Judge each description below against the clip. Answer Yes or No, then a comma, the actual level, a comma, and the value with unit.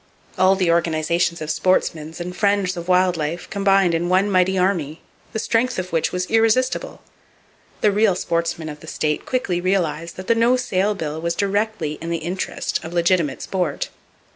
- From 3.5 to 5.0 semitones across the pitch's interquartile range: No, average, 2.9 semitones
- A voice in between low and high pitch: Yes, medium, 180 Hz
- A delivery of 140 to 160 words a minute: No, average, 175 wpm